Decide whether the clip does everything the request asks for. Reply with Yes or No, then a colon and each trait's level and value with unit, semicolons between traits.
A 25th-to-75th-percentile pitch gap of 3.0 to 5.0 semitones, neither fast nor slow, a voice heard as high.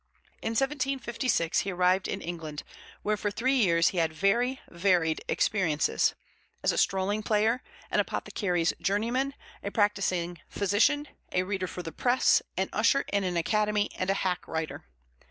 Yes: average, 4.2 semitones; average, 155 wpm; high, 200 Hz